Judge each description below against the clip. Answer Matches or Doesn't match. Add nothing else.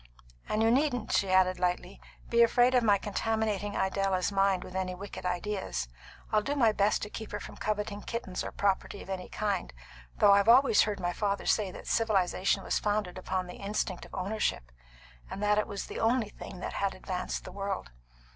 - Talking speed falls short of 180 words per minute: Doesn't match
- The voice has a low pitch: Doesn't match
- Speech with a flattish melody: Matches